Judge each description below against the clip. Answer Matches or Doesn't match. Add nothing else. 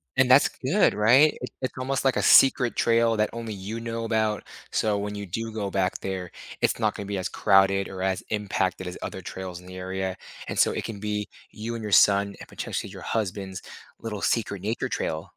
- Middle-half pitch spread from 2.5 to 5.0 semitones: Matches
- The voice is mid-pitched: Doesn't match